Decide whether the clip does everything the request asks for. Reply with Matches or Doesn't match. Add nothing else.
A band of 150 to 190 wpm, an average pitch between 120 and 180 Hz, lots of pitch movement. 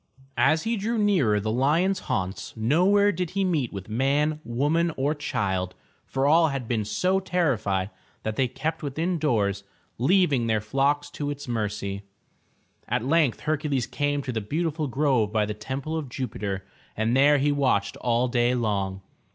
Matches